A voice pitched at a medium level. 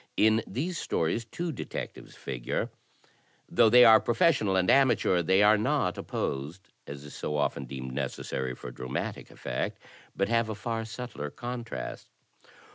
No: low, 105 Hz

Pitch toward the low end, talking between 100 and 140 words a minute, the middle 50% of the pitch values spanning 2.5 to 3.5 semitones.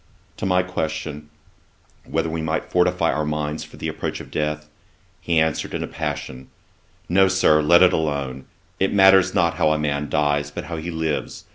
No: very low, 80 Hz; average, 185 wpm; average, 2.8 semitones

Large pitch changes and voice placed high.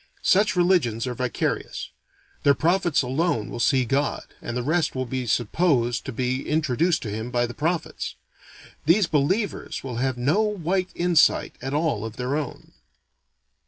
No: wide, 5.8 semitones; medium, 140 Hz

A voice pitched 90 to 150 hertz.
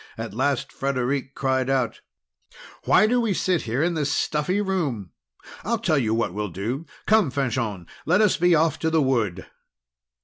Yes: medium, 140 Hz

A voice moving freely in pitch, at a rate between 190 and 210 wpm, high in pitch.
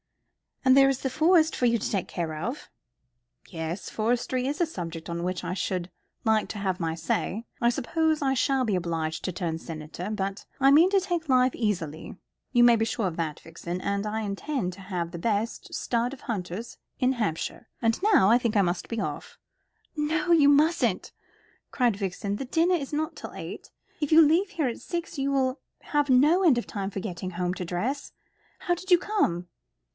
Yes: wide, 7.6 semitones; average, 200 wpm; high, 230 Hz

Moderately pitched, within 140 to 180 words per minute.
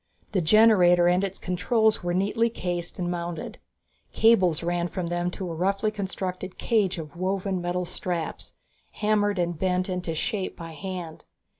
Yes: medium, 180 Hz; average, 155 wpm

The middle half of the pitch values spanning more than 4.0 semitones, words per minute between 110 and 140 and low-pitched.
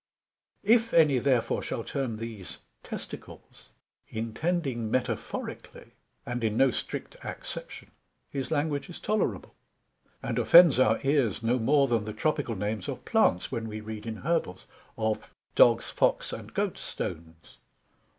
Yes: average, 4.7 semitones; slow, 135 wpm; low, 120 Hz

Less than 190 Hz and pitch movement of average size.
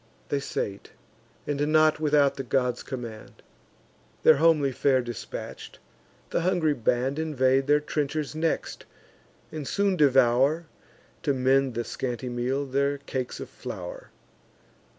Yes: medium, 140 Hz; average, 3.2 semitones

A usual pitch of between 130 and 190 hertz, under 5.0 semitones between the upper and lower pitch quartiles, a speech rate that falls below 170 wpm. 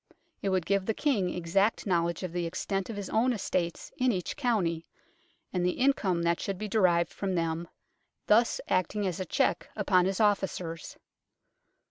No: medium, 185 Hz; average, 3.2 semitones; average, 175 wpm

